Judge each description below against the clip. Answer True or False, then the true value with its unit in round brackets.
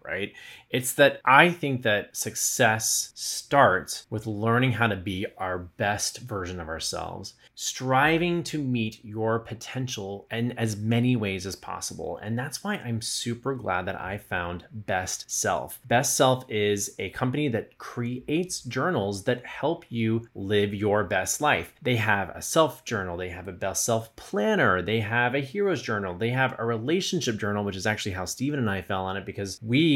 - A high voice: False (115 Hz)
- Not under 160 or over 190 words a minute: True (175 wpm)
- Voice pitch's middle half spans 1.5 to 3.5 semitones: False (4.3 semitones)